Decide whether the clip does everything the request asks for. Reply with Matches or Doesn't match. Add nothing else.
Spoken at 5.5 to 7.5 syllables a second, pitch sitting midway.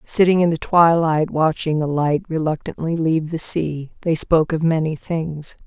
Doesn't match